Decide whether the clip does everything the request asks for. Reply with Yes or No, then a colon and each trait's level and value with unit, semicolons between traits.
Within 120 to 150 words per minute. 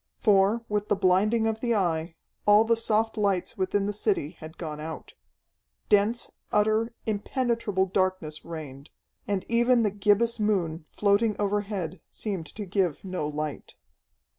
Yes: average, 140 wpm